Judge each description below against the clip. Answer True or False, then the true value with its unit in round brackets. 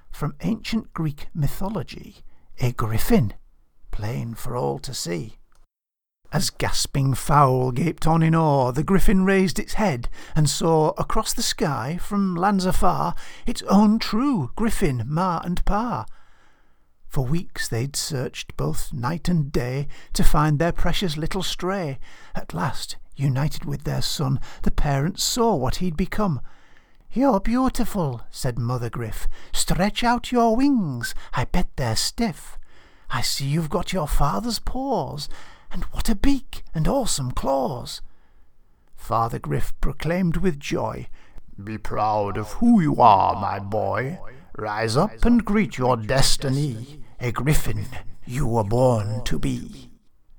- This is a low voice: False (150 Hz)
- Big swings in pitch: True (7.7 semitones)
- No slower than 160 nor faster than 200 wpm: False (140 wpm)